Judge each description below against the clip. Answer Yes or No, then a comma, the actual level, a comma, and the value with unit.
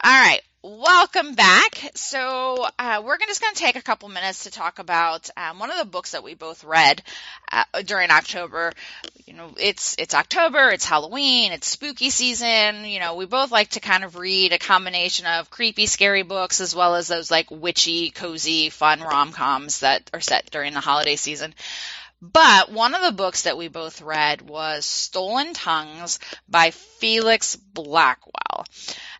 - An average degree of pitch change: No, wide, 6.1 semitones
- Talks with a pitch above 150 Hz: Yes, medium, 185 Hz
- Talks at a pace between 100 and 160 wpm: No, average, 175 wpm